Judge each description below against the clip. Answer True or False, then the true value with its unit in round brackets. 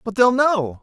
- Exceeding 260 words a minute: False (220 wpm)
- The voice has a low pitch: False (220 Hz)